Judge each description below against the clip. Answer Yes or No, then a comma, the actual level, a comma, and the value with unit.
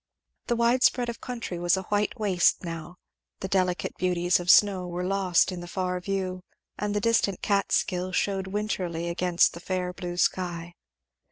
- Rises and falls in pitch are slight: Yes, narrow, 2.2 semitones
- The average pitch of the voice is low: No, medium, 185 Hz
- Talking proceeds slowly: No, average, 175 wpm